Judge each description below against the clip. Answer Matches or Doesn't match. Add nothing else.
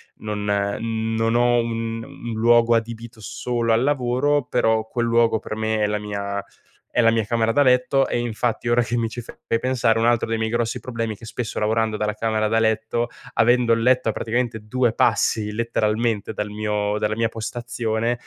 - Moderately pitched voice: Doesn't match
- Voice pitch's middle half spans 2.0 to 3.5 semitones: Doesn't match